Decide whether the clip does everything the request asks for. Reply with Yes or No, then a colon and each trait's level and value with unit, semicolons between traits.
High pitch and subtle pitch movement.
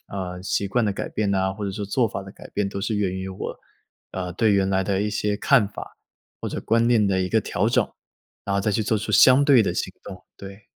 No: low, 100 Hz; narrow, 2.1 semitones